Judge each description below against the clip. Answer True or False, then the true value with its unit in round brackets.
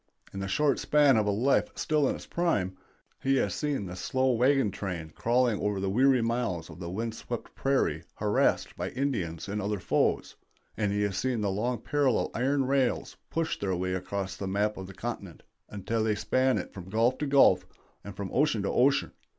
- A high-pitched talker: False (110 Hz)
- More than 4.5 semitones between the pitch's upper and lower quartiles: True (5.2 semitones)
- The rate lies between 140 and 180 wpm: False (200 wpm)